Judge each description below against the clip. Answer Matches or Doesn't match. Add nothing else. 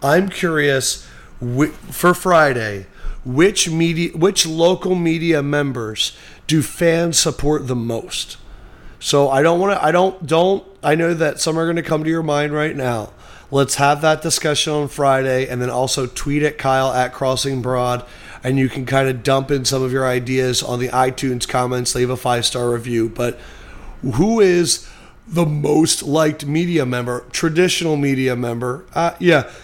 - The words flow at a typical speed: Matches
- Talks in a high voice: Doesn't match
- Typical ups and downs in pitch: Matches